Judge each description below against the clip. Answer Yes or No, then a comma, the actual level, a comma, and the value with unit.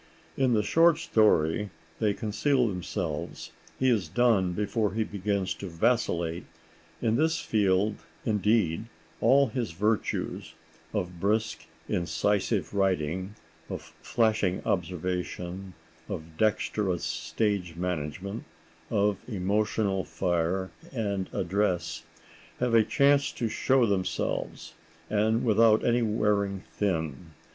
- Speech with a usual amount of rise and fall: Yes, average, 3.7 semitones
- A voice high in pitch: No, low, 100 Hz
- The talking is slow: Yes, slow, 100 wpm